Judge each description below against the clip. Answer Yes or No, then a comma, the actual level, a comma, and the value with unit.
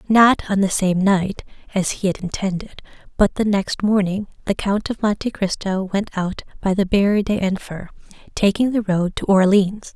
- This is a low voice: No, high, 195 Hz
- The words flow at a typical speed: Yes, average, 175 wpm